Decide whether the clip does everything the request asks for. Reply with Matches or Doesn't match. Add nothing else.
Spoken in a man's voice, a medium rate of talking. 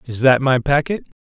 Matches